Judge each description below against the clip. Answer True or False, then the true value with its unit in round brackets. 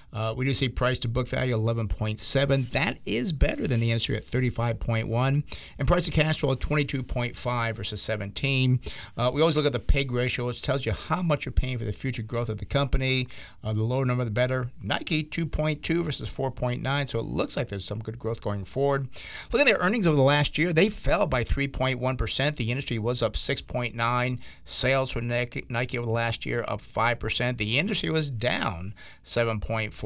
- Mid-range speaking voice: False (125 Hz)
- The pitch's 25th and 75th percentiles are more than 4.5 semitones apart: False (3.4 semitones)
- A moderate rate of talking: False (240 wpm)